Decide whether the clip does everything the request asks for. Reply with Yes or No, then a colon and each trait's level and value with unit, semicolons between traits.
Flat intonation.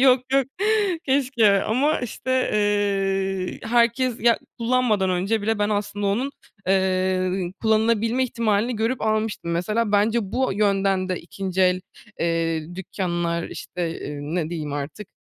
No: average, 3.8 semitones